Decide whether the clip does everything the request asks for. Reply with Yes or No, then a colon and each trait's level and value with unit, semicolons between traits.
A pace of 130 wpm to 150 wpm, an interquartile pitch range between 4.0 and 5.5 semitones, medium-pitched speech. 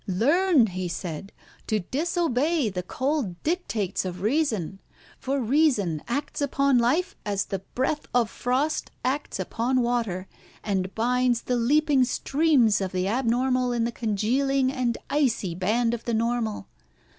No: average, 140 wpm; average, 5.2 semitones; high, 240 Hz